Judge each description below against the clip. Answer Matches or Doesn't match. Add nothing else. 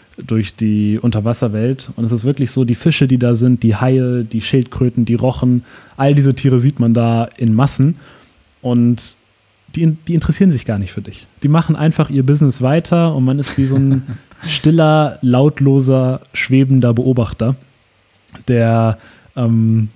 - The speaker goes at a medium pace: Matches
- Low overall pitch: Matches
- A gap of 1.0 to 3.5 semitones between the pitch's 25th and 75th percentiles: Matches